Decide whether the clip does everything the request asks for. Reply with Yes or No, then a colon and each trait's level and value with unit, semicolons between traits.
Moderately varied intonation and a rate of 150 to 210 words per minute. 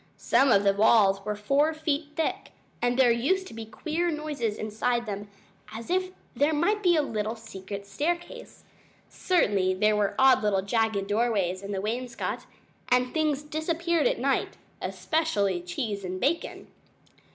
No: wide, 7.1 semitones; average, 155 wpm